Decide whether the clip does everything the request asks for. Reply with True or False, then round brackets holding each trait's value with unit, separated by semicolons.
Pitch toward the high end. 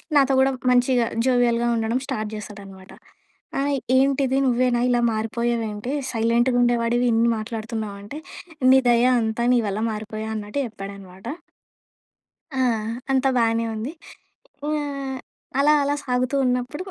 True (235 Hz)